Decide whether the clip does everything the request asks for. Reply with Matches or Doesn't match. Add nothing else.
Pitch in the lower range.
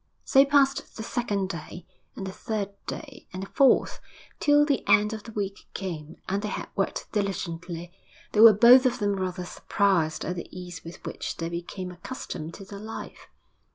Doesn't match